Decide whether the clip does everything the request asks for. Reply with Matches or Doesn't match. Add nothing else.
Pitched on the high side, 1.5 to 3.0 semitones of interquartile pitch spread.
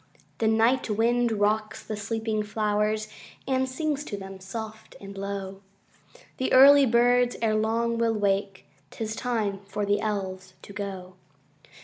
Matches